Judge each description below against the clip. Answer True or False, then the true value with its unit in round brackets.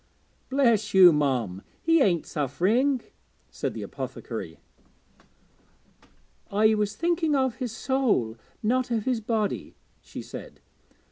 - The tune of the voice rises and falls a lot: True (6.0 semitones)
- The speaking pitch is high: True (220 Hz)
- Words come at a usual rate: False (115 wpm)